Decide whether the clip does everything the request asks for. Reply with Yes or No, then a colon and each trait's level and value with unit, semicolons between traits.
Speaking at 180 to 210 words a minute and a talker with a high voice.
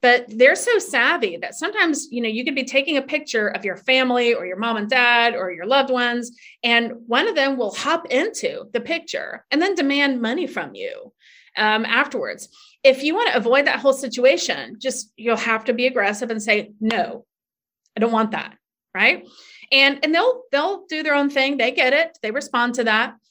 Yes: fast, 205 wpm; very high, 255 Hz